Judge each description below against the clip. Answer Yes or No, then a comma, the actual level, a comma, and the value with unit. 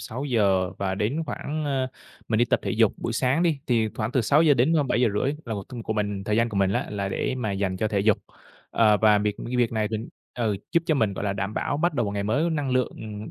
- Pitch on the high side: No, low, 110 Hz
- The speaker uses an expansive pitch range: No, average, 4.2 semitones